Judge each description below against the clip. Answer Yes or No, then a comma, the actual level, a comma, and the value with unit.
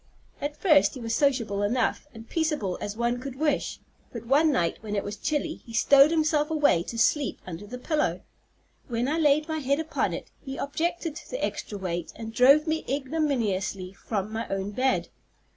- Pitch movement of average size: No, wide, 6.0 semitones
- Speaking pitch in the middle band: No, very high, 265 Hz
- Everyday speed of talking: Yes, average, 190 wpm